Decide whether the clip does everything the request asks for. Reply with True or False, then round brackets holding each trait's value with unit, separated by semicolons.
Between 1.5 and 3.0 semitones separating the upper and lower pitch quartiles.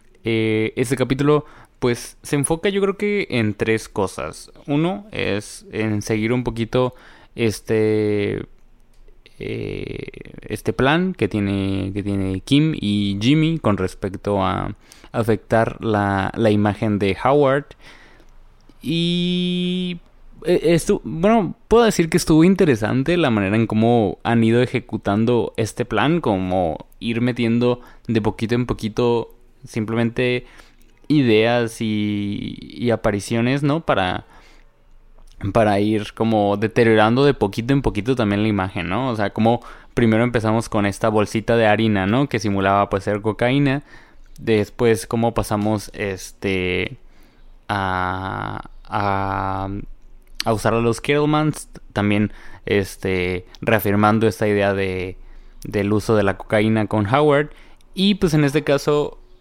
False (4.0 semitones)